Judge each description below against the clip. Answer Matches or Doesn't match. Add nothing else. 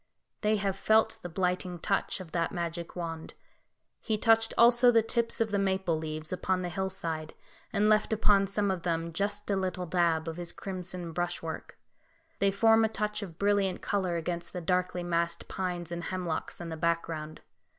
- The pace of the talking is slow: Doesn't match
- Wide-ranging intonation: Doesn't match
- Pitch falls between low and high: Matches